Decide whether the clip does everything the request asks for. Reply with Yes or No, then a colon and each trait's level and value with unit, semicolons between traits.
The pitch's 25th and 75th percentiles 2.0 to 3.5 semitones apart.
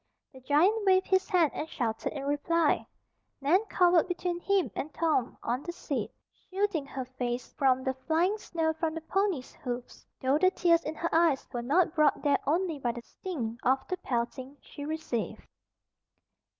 No: average, 5.1 semitones